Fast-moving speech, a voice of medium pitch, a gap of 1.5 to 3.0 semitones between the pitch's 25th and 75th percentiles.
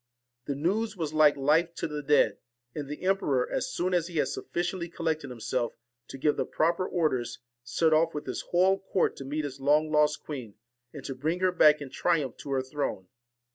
No: fast, 215 wpm; medium, 150 Hz; average, 3.6 semitones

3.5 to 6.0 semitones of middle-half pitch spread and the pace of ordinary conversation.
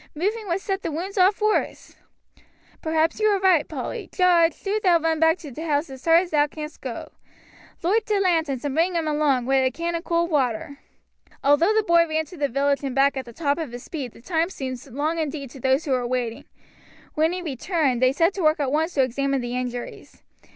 No: average, 4.0 semitones; fast, 225 wpm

